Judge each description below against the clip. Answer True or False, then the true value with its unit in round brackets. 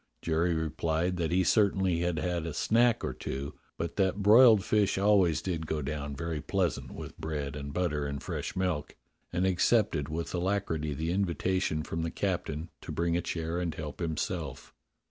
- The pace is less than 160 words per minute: False (175 wpm)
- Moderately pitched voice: False (85 Hz)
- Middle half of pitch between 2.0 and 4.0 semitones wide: True (3.1 semitones)